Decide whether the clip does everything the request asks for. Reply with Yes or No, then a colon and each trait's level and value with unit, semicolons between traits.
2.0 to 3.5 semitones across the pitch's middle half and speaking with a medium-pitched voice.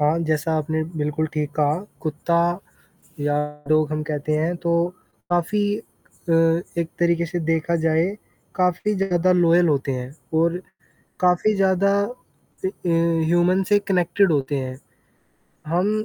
Yes: average, 2.7 semitones; medium, 170 Hz